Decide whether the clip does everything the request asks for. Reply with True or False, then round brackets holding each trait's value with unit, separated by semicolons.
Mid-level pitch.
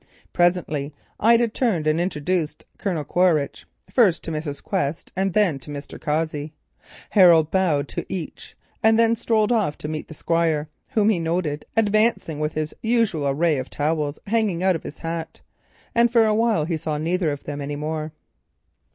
True (165 Hz)